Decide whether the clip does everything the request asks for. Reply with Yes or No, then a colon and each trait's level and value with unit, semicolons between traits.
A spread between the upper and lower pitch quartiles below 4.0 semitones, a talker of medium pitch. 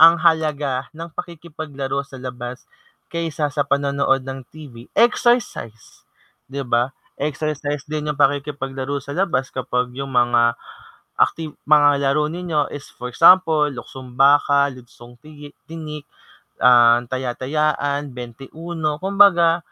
Yes: average, 3.1 semitones; medium, 145 Hz